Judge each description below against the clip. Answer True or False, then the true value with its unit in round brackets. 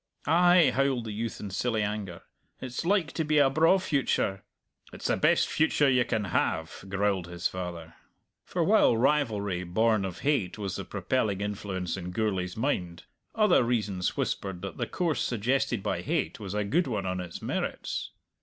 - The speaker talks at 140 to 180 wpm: True (175 wpm)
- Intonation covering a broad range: True (6.4 semitones)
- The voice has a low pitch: True (105 Hz)